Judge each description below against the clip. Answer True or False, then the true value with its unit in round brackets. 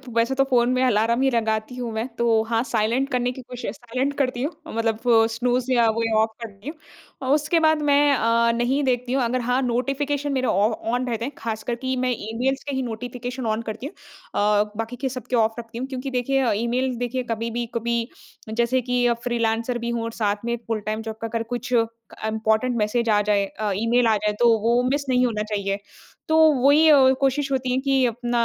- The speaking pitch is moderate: False (240 Hz)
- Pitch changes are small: True (2.3 semitones)